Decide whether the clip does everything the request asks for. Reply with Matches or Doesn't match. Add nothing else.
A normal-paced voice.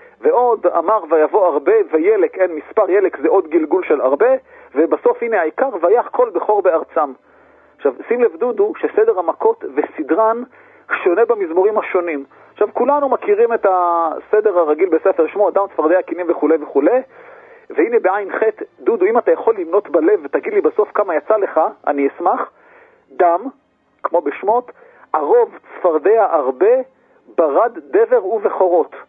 Matches